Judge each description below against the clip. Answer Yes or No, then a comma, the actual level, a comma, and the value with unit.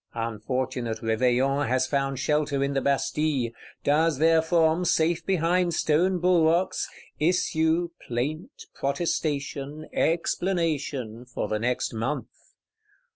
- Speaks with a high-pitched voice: No, medium, 150 Hz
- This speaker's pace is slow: Yes, slow, 100 wpm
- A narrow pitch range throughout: No, average, 4.2 semitones